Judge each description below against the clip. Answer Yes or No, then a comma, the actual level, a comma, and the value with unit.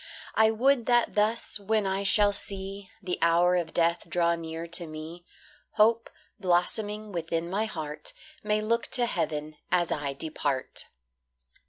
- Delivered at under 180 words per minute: Yes, average, 145 wpm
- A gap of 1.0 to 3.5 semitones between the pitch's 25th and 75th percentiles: No, average, 4.4 semitones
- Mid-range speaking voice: Yes, medium, 180 Hz